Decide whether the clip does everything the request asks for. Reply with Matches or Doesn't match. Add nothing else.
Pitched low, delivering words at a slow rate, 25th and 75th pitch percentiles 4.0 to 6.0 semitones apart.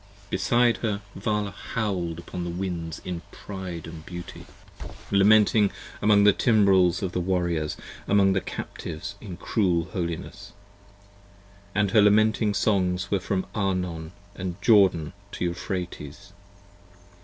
Doesn't match